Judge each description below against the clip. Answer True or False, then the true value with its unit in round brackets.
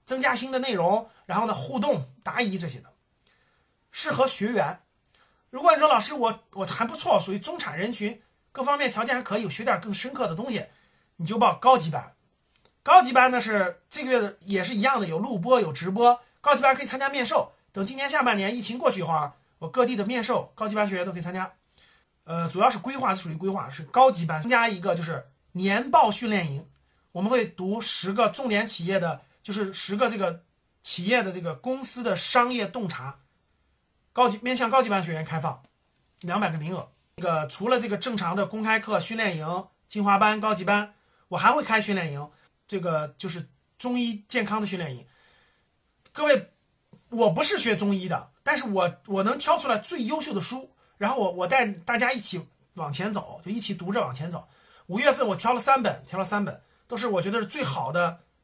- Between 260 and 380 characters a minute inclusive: True (300 characters per minute)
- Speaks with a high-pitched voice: True (205 Hz)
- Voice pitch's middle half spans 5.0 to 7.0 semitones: True (5.3 semitones)